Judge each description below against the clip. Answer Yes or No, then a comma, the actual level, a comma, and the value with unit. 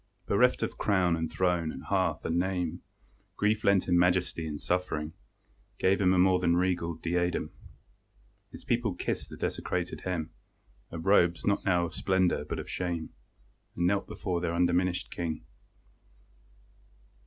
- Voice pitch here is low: Yes, very low, 90 Hz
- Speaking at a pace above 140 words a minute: Yes, average, 150 wpm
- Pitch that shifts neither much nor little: No, narrow, 1.6 semitones